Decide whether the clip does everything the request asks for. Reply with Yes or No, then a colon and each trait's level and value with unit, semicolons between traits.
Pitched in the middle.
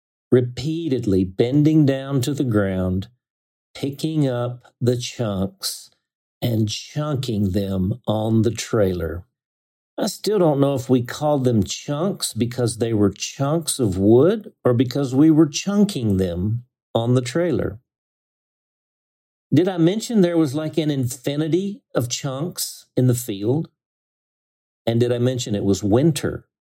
No: low, 125 Hz